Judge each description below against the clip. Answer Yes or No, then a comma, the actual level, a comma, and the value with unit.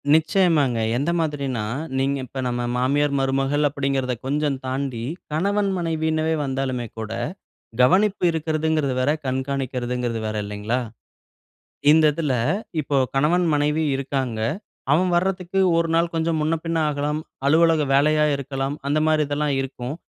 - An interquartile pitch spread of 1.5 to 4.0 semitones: Yes, average, 3.2 semitones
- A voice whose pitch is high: No, medium, 145 Hz